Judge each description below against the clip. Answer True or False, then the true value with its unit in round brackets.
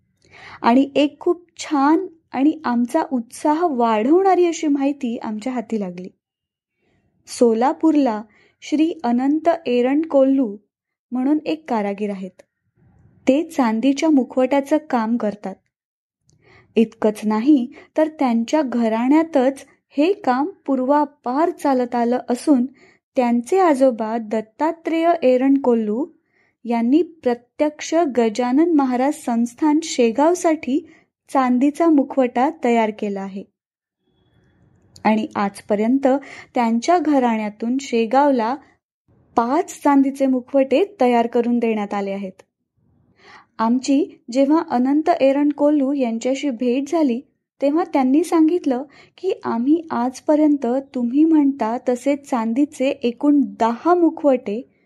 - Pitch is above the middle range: True (270 Hz)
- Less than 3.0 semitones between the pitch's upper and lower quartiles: False (4.2 semitones)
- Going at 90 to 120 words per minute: True (95 wpm)